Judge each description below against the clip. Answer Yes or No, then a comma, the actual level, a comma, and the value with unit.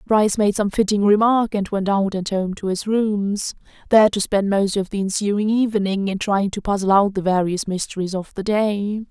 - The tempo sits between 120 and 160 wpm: No, fast, 205 wpm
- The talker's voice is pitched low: No, high, 200 Hz